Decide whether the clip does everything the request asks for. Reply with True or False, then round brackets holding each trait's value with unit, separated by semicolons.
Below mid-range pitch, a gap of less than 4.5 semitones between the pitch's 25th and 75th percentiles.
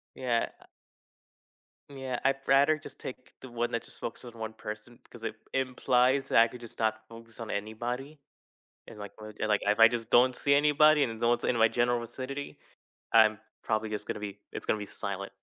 True (120 Hz; 2.9 semitones)